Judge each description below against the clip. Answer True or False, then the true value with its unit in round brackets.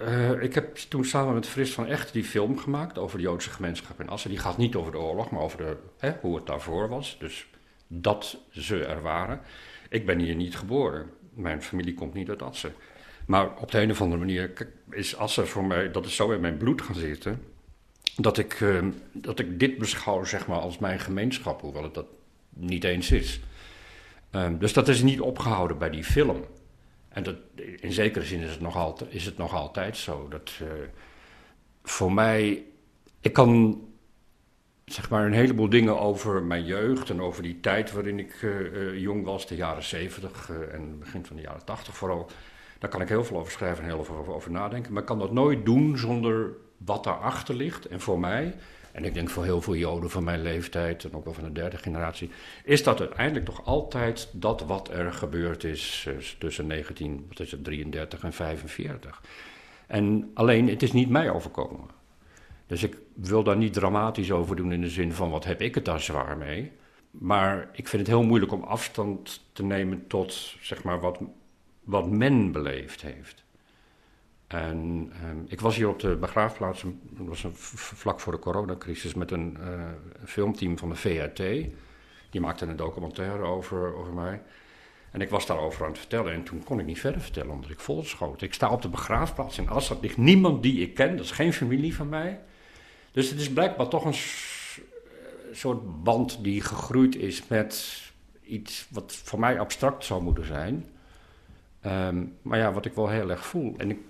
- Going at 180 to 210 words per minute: True (195 wpm)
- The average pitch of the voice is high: False (95 Hz)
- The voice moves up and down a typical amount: True (4.6 semitones)